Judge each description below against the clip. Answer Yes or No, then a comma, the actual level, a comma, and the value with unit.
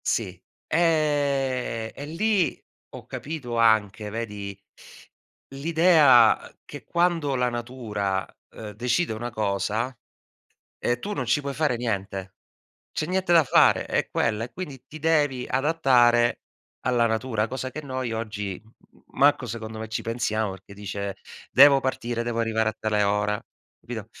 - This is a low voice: Yes, low, 120 Hz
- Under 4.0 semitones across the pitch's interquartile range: No, average, 4.4 semitones